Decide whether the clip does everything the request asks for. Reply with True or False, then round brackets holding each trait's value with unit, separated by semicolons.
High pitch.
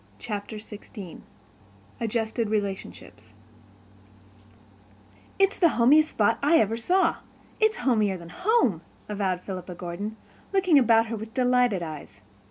True (220 Hz)